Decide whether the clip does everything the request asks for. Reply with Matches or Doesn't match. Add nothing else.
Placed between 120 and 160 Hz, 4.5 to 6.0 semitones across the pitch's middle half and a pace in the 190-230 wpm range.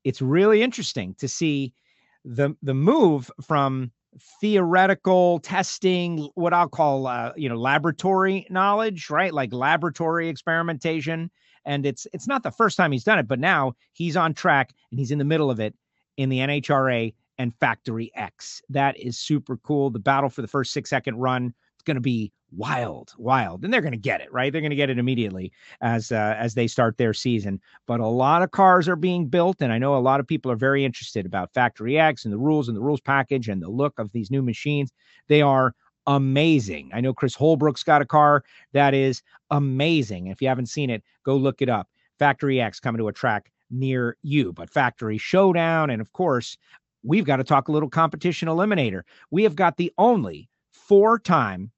Matches